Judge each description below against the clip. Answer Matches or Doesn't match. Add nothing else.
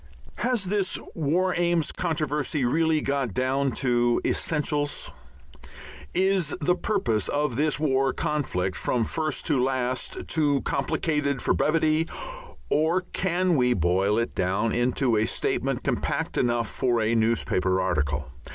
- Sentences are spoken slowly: Matches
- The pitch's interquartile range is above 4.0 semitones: Matches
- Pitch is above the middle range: Doesn't match